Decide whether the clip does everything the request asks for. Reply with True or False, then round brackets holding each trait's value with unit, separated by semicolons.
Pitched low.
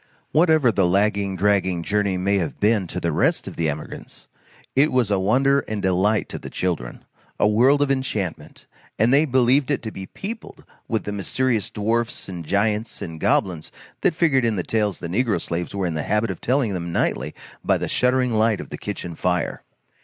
True (105 Hz)